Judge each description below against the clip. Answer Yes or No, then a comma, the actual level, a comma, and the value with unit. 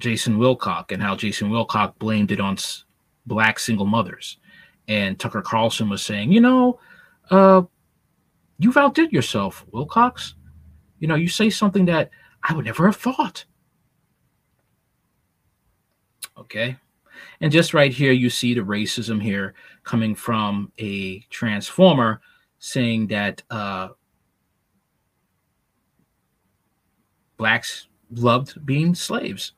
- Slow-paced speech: Yes, slow, 115 wpm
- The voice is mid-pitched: No, low, 120 Hz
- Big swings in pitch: Yes, wide, 8.2 semitones